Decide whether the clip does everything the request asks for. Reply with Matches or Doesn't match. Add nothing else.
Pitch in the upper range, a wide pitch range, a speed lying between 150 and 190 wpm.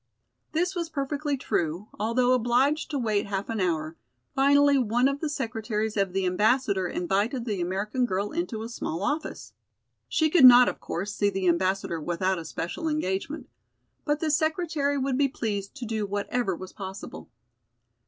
Matches